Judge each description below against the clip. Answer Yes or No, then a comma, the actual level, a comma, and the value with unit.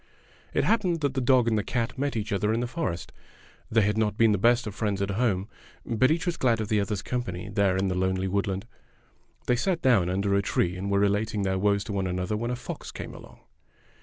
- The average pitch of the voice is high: No, low, 105 Hz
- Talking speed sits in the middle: No, fast, 235 wpm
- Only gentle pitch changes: No, average, 3.7 semitones